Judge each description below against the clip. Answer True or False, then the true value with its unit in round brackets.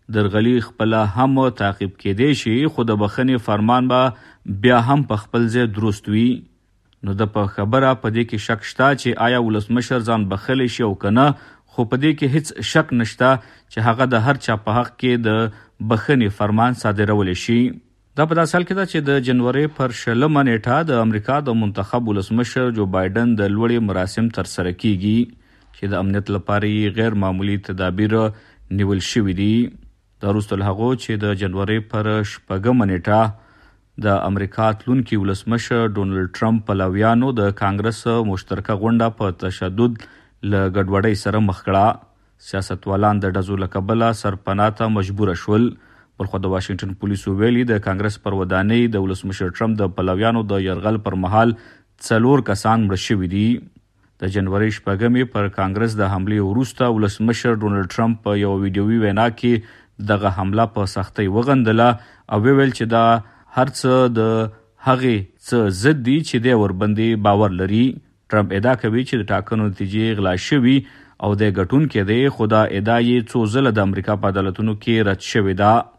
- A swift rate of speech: False (165 wpm)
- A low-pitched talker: True (110 Hz)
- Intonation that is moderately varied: True (3.1 semitones)